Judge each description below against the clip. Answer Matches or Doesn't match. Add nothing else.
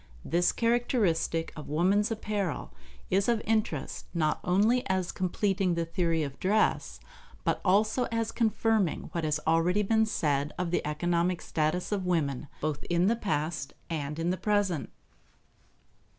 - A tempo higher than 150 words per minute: Doesn't match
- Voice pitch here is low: Doesn't match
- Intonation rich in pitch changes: Doesn't match